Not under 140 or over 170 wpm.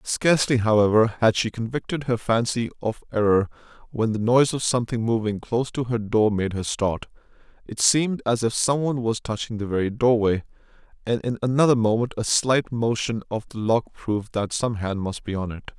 No: average, 185 wpm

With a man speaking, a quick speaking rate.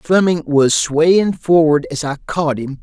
No: male; average, 170 wpm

